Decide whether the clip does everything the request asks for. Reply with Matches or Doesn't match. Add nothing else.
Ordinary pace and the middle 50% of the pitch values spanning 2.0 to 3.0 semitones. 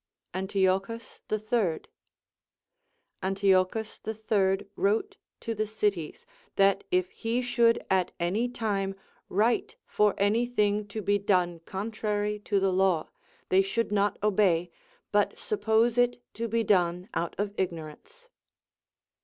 Doesn't match